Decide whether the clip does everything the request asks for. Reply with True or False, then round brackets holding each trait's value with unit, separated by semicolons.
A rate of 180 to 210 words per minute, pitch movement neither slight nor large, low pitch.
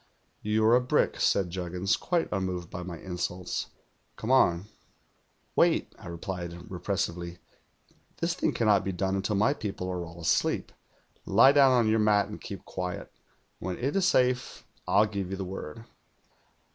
False (160 wpm; 4.0 semitones; 95 Hz)